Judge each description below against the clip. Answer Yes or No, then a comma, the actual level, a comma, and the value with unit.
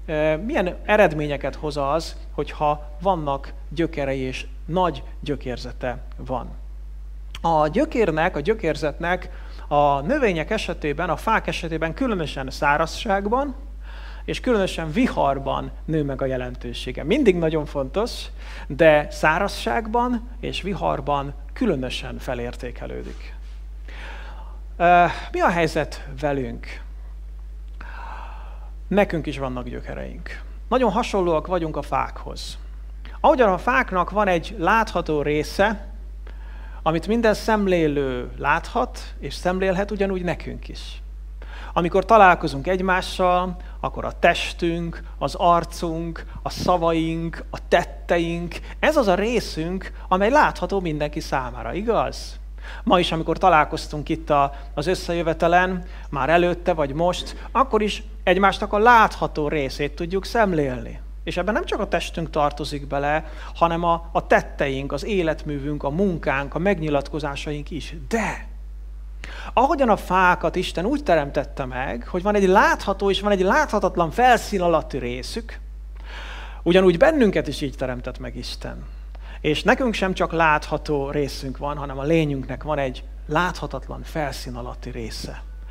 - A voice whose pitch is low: No, medium, 155 Hz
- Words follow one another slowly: Yes, slow, 120 wpm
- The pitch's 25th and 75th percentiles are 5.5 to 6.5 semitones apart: No, average, 5.1 semitones